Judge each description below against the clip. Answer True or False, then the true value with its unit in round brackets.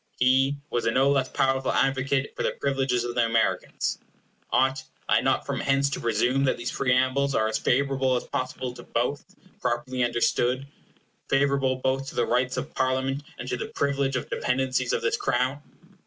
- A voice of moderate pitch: False (130 Hz)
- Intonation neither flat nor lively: False (1.6 semitones)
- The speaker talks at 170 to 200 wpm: True (185 wpm)